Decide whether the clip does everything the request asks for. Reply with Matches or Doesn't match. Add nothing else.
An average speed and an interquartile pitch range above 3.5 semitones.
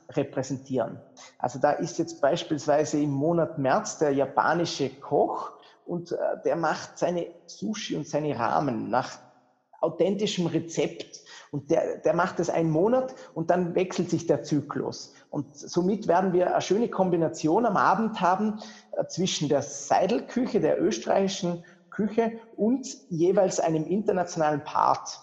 Matches